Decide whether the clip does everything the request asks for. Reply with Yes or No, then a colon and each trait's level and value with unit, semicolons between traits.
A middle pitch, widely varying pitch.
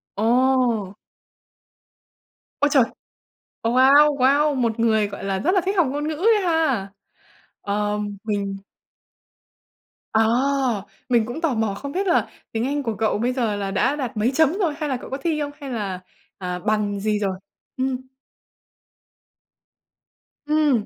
No: high, 245 Hz; wide, 5.7 semitones